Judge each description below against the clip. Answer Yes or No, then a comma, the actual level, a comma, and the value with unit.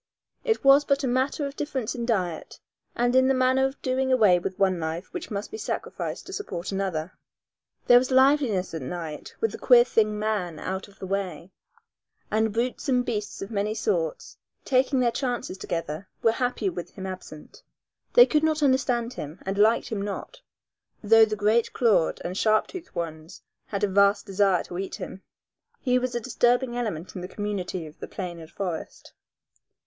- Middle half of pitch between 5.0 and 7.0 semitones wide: Yes, wide, 5.4 semitones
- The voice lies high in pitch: Yes, high, 215 Hz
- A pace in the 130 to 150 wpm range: No, average, 185 wpm